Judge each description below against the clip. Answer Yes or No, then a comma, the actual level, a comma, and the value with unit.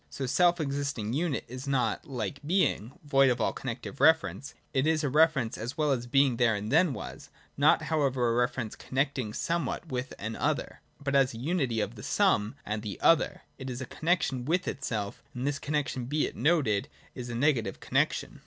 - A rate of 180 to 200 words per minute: Yes, average, 190 wpm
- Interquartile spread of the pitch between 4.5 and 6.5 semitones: No, average, 3.9 semitones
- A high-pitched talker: No, low, 135 Hz